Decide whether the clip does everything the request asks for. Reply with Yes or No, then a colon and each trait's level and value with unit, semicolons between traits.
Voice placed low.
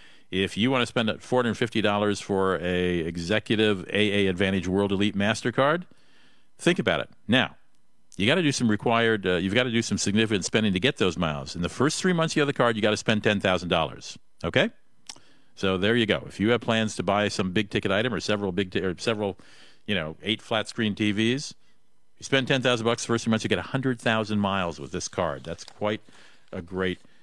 Yes: low, 105 Hz